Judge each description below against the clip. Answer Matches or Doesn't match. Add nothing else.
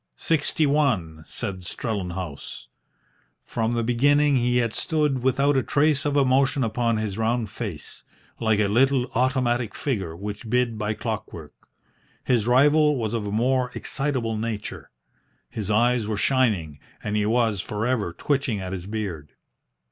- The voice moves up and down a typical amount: Matches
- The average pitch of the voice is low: Matches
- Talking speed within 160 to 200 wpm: Doesn't match